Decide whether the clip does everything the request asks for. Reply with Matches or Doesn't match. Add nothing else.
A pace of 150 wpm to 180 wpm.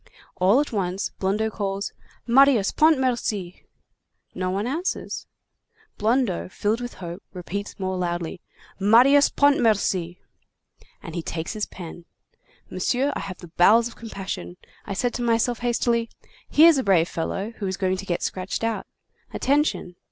Doesn't match